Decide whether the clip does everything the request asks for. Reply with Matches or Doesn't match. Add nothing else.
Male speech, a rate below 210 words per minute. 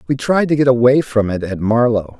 Doesn't match